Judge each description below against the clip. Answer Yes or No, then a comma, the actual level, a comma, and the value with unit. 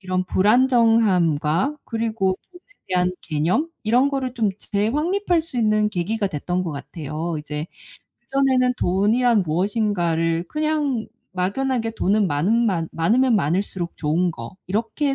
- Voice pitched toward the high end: Yes, high, 210 Hz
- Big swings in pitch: Yes, wide, 6.1 semitones